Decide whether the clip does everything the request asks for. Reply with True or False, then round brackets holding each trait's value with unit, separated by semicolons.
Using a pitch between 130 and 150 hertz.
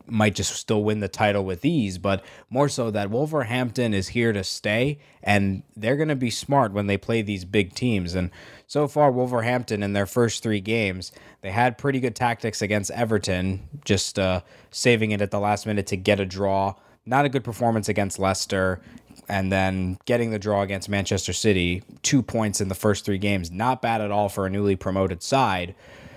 False (105 Hz)